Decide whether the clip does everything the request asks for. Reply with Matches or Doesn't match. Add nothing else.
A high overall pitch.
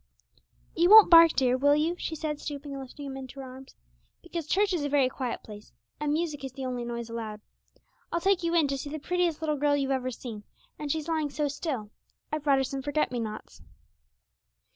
Matches